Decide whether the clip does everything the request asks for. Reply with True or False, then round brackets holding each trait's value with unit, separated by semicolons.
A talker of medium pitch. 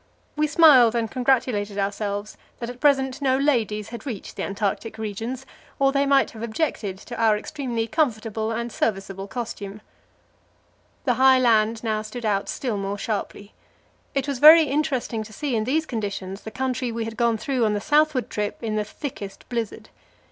False (230 Hz)